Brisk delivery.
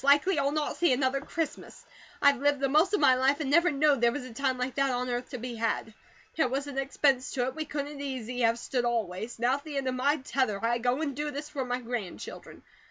Yes: fast, 245 wpm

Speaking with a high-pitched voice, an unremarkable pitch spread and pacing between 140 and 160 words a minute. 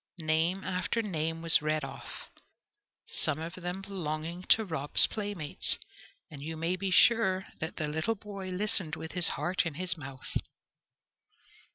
No: medium, 170 Hz; average, 3.3 semitones; average, 150 wpm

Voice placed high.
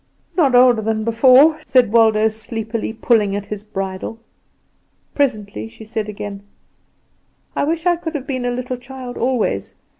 Yes: high, 230 Hz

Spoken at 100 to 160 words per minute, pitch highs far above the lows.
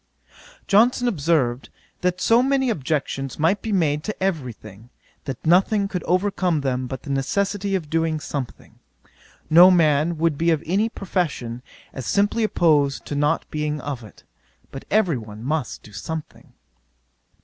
Yes: average, 150 wpm; wide, 5.7 semitones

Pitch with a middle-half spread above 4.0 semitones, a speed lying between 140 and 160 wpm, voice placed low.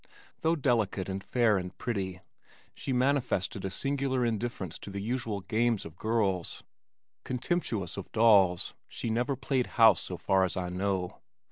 Yes: average, 4.5 semitones; average, 150 wpm; low, 110 Hz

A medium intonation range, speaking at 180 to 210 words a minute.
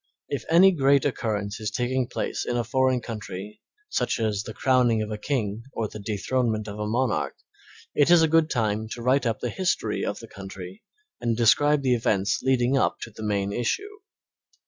Yes: average, 3.7 semitones; average, 190 wpm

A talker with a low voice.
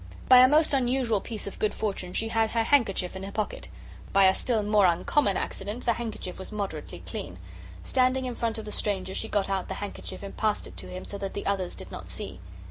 No: high, 210 Hz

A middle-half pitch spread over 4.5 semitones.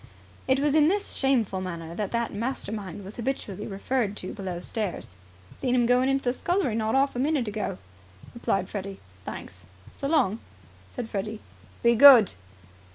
Yes: average, 5.2 semitones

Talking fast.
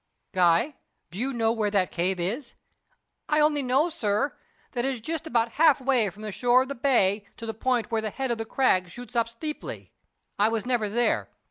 Yes: fast, 215 wpm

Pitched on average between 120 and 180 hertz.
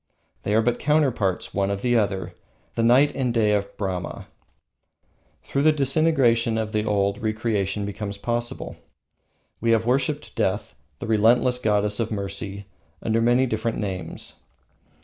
No: low, 110 Hz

